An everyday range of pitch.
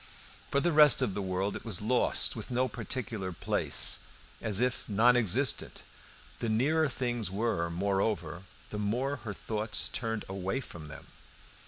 Yes: average, 4.4 semitones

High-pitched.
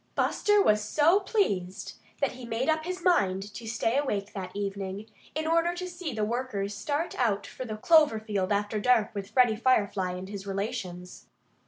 Yes: high, 220 Hz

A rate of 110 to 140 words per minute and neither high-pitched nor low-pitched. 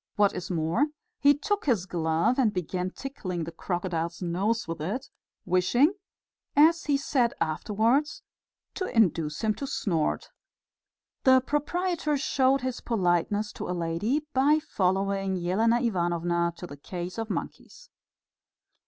No: slow, 135 wpm; high, 205 Hz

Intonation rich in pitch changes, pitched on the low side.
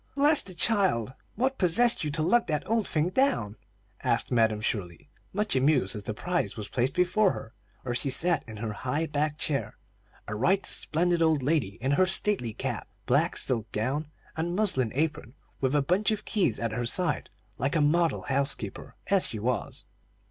No: wide, 7.0 semitones; medium, 150 Hz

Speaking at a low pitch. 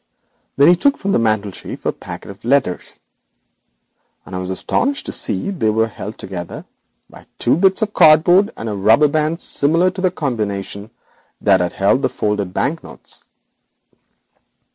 Yes: low, 120 Hz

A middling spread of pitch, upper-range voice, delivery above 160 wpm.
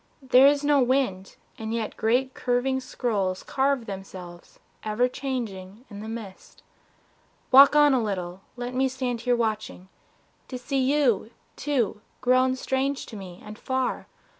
No: average, 3.9 semitones; high, 245 Hz; average, 145 wpm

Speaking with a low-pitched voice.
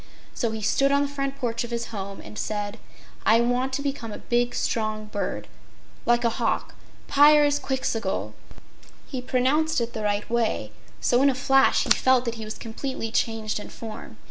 No: high, 235 Hz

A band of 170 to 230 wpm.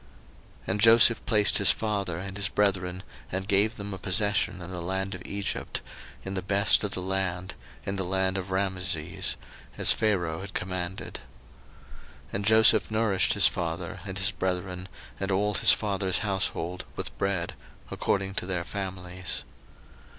No: average, 160 wpm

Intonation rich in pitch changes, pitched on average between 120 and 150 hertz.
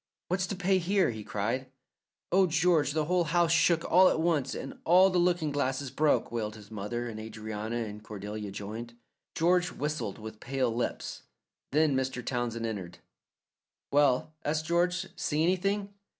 Yes: wide, 7.5 semitones; medium, 140 Hz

